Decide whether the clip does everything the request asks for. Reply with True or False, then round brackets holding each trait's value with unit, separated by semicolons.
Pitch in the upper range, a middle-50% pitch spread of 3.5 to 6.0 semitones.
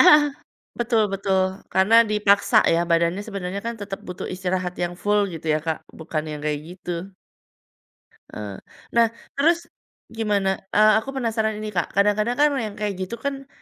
True (200 Hz; 3.8 semitones)